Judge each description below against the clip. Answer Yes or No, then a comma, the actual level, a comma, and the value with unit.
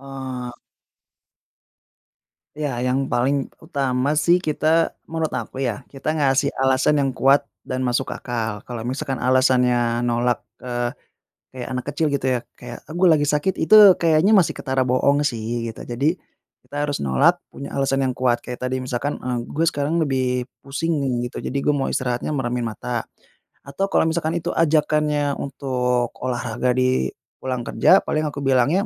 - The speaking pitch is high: No, low, 135 Hz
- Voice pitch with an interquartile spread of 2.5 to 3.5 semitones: Yes, average, 3.0 semitones